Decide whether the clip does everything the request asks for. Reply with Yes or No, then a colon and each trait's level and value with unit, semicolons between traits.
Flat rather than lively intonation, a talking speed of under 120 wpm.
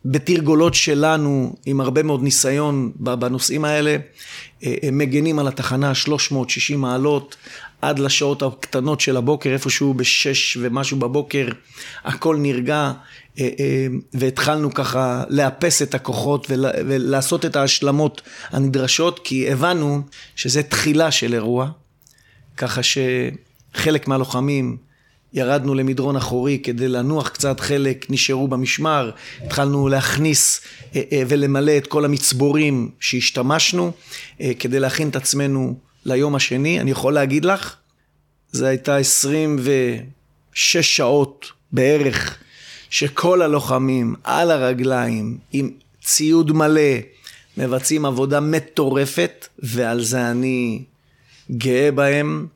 Yes: narrow, 2.2 semitones; slow, 100 wpm